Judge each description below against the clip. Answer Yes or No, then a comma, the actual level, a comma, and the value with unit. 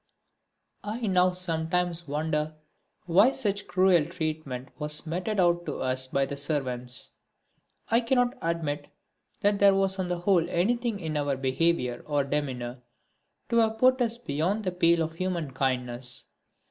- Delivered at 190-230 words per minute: No, average, 145 wpm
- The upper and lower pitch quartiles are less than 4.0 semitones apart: No, average, 5.2 semitones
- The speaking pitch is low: No, medium, 170 Hz